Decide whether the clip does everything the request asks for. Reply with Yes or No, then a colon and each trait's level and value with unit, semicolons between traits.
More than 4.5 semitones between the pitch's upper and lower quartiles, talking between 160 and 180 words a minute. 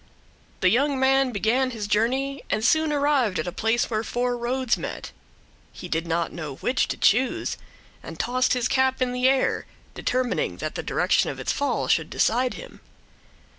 No: average, 3.3 semitones; average, 175 wpm